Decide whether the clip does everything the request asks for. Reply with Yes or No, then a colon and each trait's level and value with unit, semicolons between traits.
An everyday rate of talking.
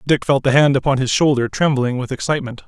No: fast, 225 wpm